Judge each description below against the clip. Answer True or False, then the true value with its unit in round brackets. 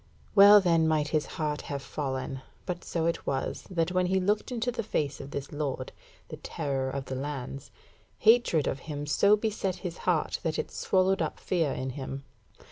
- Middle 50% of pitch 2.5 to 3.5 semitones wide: False (5.1 semitones)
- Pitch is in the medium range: True (155 Hz)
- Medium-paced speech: True (190 wpm)